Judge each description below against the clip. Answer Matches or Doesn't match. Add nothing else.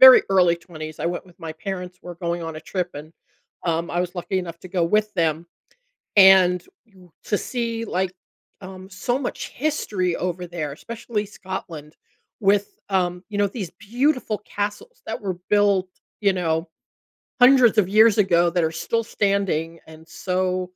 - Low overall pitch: Doesn't match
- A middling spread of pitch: Matches